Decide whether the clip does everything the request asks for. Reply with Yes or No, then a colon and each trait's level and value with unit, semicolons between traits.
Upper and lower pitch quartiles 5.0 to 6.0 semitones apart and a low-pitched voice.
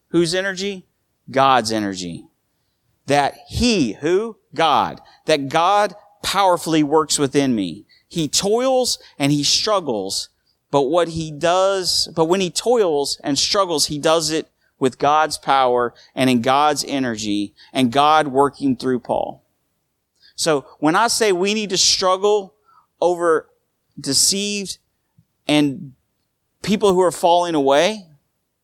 No: wide, 5.6 semitones; medium, 155 Hz